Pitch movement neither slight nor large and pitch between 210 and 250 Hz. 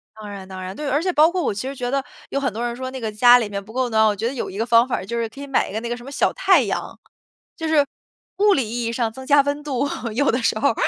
Yes: average, 4.1 semitones; high, 245 Hz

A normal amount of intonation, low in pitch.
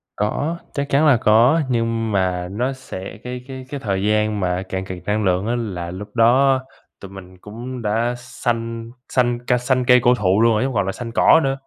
Yes: average, 3.9 semitones; low, 115 Hz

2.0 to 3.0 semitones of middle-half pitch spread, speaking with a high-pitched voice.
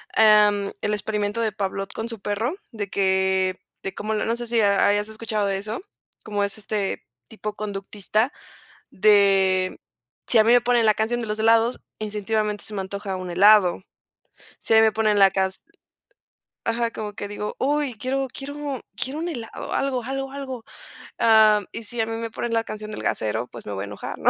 Yes: narrow, 2.4 semitones; high, 215 Hz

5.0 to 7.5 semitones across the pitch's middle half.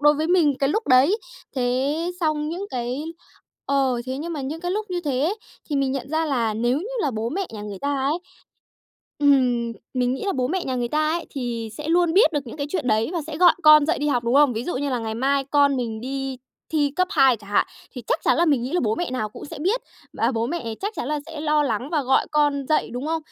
No: average, 4.0 semitones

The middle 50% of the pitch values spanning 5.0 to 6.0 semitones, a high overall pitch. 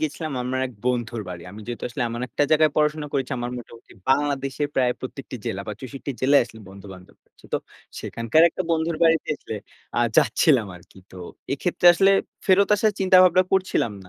No: average, 5.3 semitones; low, 135 Hz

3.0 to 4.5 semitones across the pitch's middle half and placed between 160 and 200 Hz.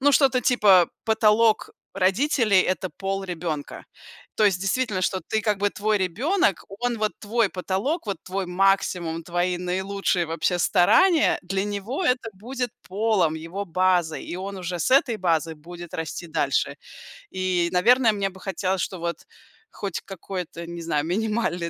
Yes: average, 3.6 semitones; high, 190 Hz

